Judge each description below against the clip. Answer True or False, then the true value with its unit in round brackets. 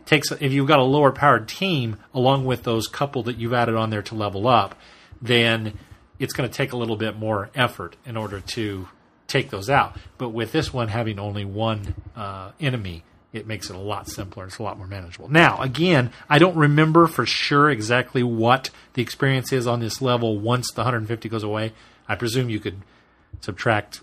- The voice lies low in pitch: True (115 Hz)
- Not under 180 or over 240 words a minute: True (200 wpm)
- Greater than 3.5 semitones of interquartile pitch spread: True (3.9 semitones)